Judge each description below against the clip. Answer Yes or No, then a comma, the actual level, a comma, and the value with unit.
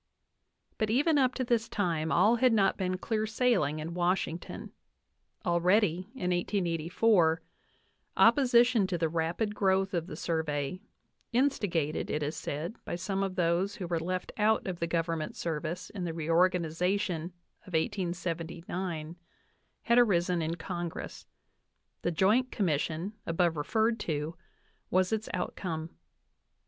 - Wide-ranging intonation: No, average, 4.0 semitones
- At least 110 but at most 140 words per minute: Yes, slow, 135 wpm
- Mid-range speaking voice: Yes, medium, 180 Hz